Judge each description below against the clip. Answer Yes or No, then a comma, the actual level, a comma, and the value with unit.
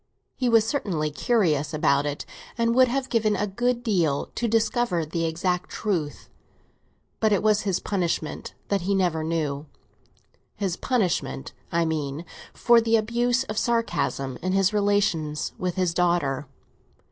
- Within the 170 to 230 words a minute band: No, average, 145 wpm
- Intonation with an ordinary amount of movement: No, wide, 6.0 semitones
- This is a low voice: No, medium, 185 Hz